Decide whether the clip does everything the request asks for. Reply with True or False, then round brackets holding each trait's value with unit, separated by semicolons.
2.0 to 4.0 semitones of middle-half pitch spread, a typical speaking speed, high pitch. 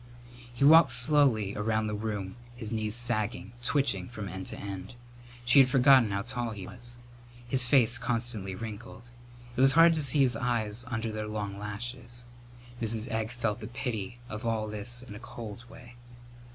False (2.5 semitones; 175 wpm; 115 Hz)